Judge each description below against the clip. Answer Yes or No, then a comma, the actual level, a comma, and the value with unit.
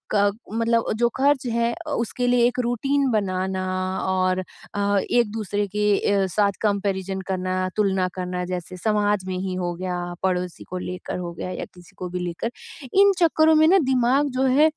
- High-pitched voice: Yes, high, 205 Hz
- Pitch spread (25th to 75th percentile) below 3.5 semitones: No, average, 4.8 semitones